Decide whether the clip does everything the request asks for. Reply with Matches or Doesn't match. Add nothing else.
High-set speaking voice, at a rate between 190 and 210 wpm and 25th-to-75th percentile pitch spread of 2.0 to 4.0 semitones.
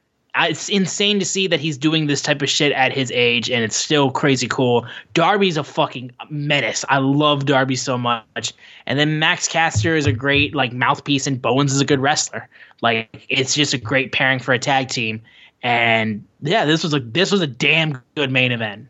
Doesn't match